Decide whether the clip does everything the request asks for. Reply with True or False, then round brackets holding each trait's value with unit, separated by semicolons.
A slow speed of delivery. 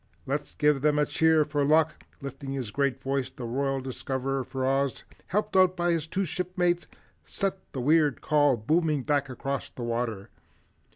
False (170 wpm)